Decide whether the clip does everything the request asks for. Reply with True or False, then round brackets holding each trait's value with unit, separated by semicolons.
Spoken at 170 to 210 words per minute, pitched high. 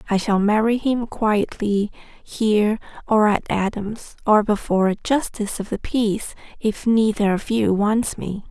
False (155 wpm; 210 Hz)